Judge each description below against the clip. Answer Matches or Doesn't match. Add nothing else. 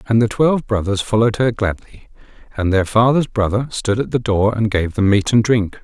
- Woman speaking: Doesn't match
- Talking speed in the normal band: Doesn't match